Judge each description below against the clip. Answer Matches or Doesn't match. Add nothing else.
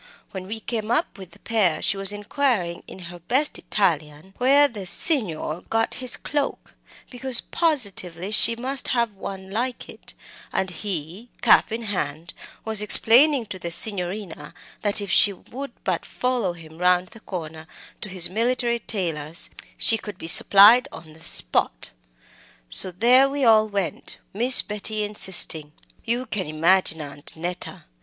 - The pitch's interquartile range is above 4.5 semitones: Matches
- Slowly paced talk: Doesn't match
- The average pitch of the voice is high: Matches